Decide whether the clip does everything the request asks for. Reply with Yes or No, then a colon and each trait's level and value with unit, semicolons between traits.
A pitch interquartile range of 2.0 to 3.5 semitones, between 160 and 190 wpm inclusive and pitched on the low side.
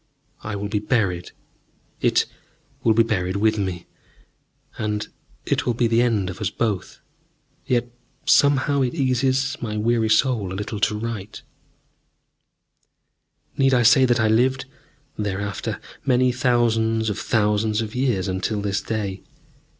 No: average, 3.0 semitones; average, 140 wpm; low, 110 Hz